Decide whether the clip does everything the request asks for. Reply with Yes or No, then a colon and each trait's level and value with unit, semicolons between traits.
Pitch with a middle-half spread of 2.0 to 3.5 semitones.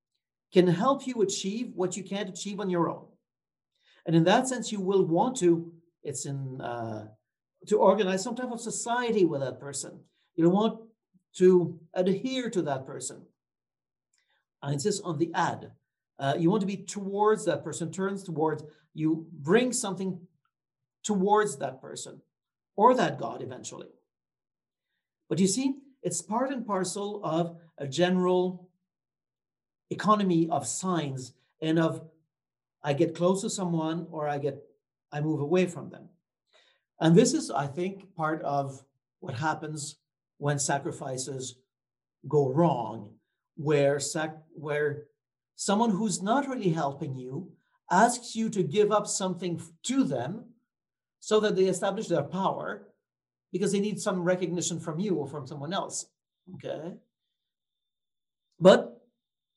No: average, 5.0 semitones